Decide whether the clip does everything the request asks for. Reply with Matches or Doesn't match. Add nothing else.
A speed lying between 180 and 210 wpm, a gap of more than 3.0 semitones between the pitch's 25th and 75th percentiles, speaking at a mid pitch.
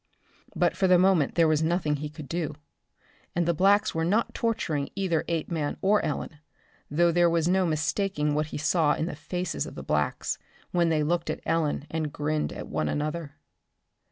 Doesn't match